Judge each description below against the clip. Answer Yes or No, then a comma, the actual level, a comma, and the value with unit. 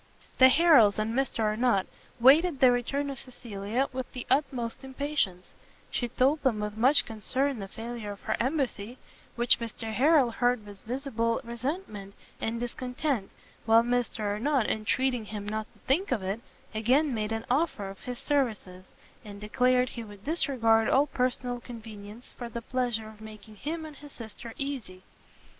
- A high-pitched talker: Yes, high, 240 Hz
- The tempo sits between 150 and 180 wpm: Yes, average, 160 wpm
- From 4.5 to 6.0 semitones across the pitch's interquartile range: No, average, 3.6 semitones